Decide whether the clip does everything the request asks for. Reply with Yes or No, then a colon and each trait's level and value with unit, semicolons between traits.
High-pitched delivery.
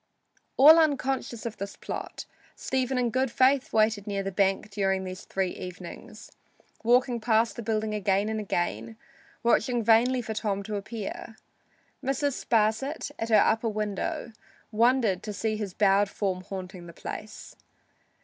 Yes: high, 215 Hz